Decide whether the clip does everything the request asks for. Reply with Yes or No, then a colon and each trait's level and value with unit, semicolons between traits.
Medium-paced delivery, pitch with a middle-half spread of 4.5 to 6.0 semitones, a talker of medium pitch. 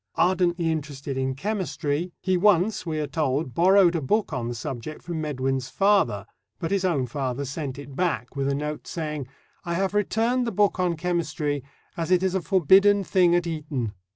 Yes: average, 185 wpm; average, 4.9 semitones; medium, 165 Hz